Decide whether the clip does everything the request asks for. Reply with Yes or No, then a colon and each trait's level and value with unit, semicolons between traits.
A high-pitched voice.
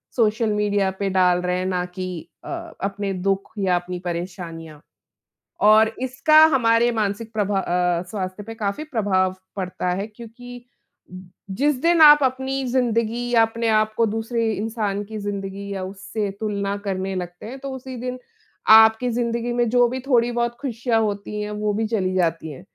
Yes: high, 210 Hz